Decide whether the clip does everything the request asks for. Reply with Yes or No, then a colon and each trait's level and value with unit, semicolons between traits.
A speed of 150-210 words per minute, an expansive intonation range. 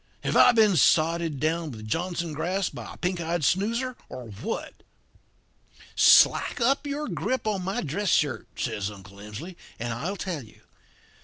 Yes: average, 160 wpm; wide, 7.3 semitones